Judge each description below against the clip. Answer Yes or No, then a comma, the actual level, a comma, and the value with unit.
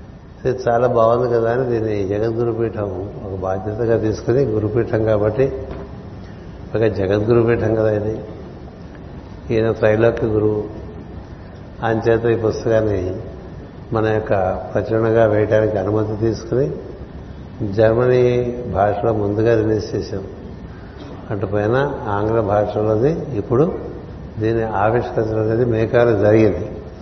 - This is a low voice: Yes, low, 110 Hz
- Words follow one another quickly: No, average, 95 wpm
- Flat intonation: Yes, narrow, 2.3 semitones